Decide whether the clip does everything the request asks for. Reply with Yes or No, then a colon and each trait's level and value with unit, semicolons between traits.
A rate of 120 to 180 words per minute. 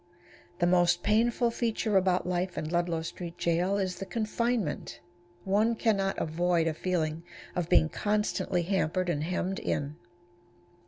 Yes: average, 145 wpm